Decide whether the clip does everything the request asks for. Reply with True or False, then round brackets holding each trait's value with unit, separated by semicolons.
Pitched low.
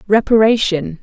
False (205 Hz)